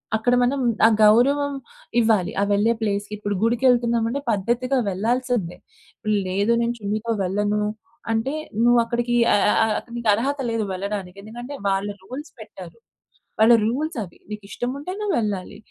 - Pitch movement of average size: Yes, average, 3.1 semitones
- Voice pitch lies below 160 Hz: No, high, 230 Hz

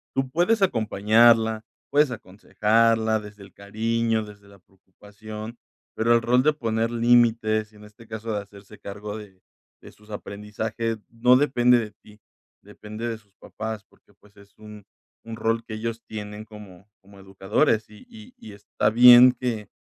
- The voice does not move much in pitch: Yes, narrow, 1.9 semitones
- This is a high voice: No, low, 110 Hz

